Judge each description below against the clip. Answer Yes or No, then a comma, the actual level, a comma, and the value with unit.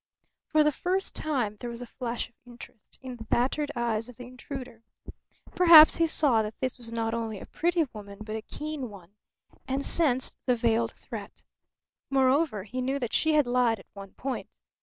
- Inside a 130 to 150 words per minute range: No, average, 190 wpm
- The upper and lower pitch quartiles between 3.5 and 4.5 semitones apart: Yes, average, 3.8 semitones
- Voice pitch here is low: No, high, 245 Hz